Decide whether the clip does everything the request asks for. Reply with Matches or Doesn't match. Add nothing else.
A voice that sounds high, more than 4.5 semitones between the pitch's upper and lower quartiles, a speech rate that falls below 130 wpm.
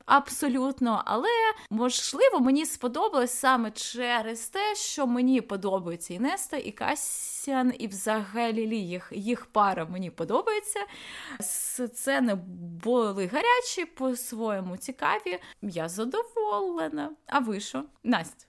Matches